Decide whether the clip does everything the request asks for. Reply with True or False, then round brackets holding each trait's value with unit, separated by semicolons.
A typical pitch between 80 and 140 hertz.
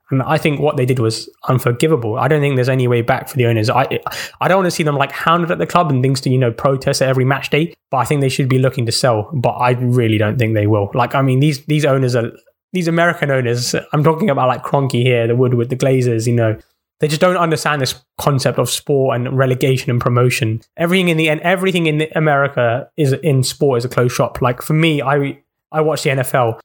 True (135 Hz)